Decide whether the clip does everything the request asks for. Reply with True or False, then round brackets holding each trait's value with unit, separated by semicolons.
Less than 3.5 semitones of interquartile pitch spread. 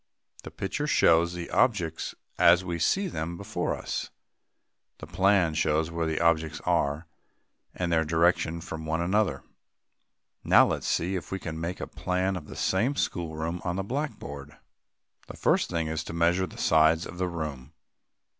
True (2.5 semitones)